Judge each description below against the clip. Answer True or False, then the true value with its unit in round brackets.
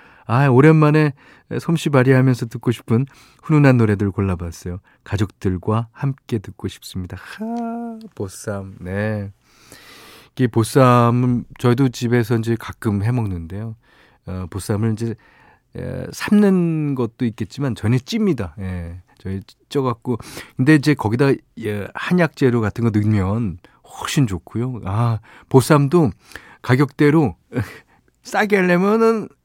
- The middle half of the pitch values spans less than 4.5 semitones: False (5.4 semitones)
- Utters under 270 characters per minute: True (250 characters per minute)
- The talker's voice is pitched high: False (120 Hz)